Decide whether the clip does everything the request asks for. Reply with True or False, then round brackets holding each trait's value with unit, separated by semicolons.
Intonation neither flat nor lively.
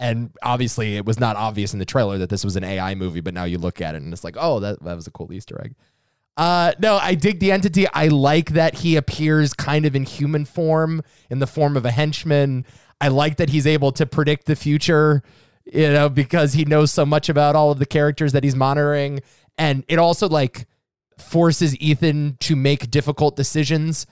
True (3.9 semitones)